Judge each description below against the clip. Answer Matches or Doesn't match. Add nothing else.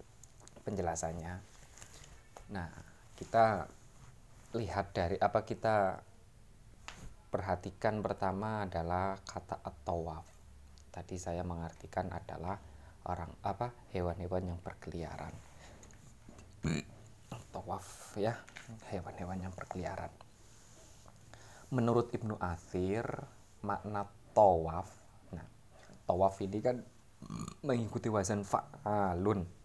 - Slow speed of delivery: Matches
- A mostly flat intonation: Doesn't match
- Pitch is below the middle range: Matches